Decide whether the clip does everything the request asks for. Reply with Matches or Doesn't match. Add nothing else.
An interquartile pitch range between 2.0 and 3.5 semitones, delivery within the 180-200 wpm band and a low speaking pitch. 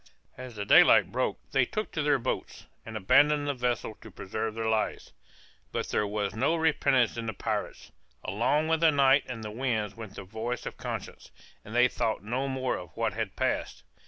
Doesn't match